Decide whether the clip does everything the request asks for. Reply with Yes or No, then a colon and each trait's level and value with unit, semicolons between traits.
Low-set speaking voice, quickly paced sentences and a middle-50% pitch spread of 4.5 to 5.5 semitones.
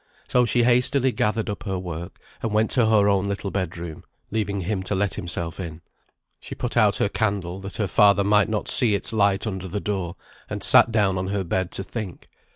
No: low, 100 Hz; fast, 215 wpm; narrow, 2.5 semitones